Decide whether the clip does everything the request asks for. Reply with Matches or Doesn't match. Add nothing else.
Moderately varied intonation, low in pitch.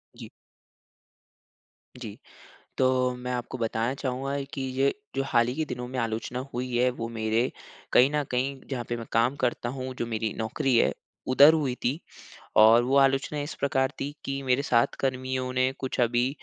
Doesn't match